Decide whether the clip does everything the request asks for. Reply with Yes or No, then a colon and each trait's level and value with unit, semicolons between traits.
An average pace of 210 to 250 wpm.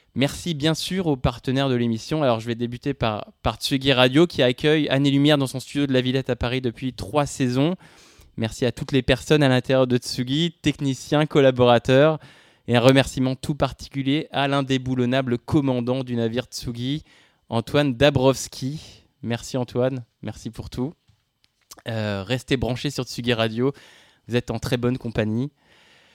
No: average, 165 wpm